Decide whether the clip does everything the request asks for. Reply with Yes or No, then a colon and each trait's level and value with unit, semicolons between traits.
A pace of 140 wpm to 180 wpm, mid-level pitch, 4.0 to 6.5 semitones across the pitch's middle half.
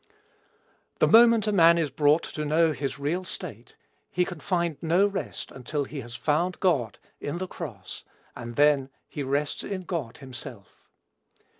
Yes: average, 160 wpm; medium, 155 Hz; average, 4.4 semitones